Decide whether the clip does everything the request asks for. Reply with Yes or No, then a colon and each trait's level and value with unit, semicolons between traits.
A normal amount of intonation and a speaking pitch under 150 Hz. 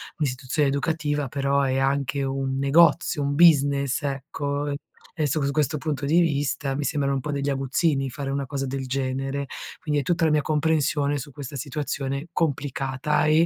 No: narrow, 1.7 semitones; medium, 140 Hz